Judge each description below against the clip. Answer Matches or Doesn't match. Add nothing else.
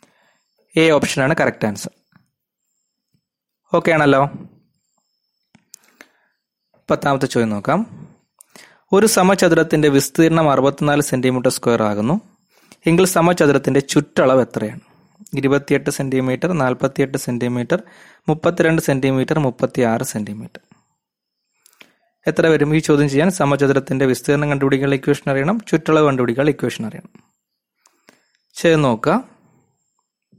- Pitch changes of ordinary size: Matches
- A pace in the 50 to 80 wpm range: Doesn't match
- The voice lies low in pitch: Doesn't match